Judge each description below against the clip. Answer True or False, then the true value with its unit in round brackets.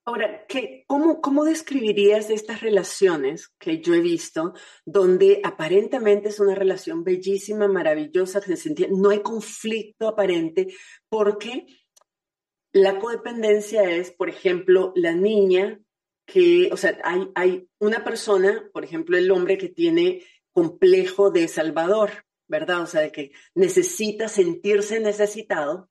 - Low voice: False (215 Hz)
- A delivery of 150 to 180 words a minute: False (130 wpm)